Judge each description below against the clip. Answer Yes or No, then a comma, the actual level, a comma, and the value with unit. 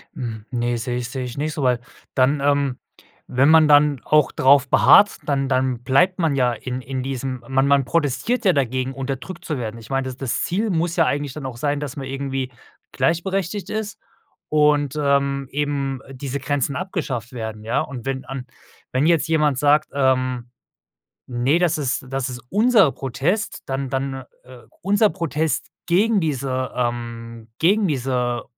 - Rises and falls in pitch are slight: No, average, 3.1 semitones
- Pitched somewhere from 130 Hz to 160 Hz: Yes, low, 135 Hz